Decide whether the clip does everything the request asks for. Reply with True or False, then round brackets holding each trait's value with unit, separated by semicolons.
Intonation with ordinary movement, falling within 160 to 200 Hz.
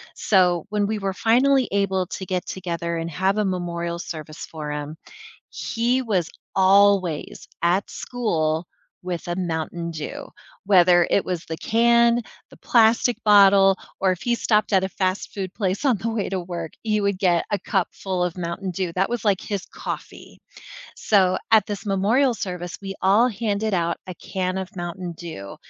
True (3.1 semitones; 190 Hz)